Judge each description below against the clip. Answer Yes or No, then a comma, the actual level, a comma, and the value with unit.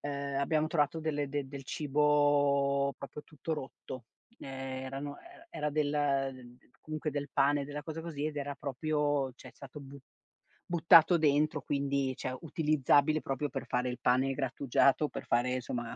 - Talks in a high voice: No, medium, 140 Hz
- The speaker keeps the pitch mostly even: Yes, narrow, 1.8 semitones